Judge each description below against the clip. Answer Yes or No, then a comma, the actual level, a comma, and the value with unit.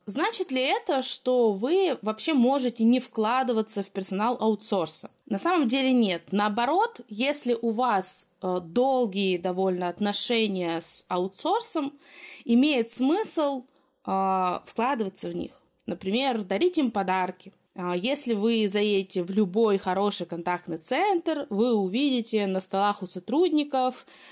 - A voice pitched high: Yes, high, 225 Hz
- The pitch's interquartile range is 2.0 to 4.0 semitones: No, wide, 5.6 semitones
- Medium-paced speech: Yes, average, 120 wpm